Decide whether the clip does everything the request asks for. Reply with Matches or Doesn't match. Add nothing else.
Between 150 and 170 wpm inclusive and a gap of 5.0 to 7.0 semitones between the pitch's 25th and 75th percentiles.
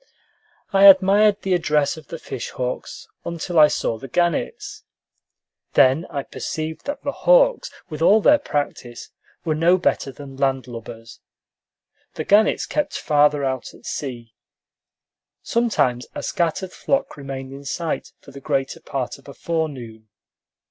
Doesn't match